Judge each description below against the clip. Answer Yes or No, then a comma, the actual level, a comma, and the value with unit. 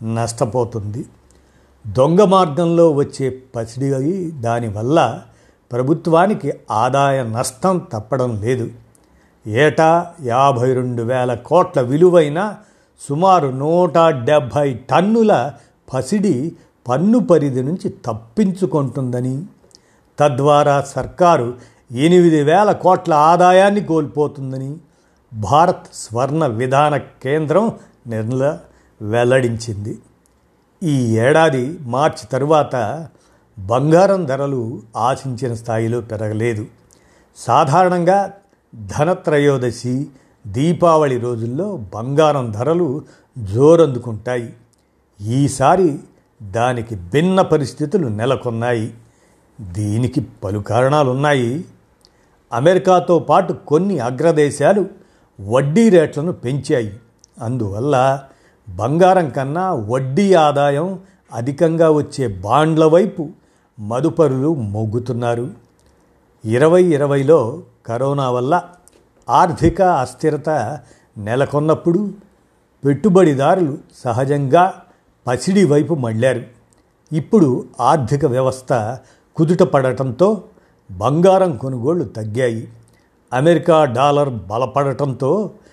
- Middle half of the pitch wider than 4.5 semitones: Yes, wide, 5.5 semitones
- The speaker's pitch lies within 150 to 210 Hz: No, medium, 140 Hz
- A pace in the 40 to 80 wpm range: Yes, average, 75 wpm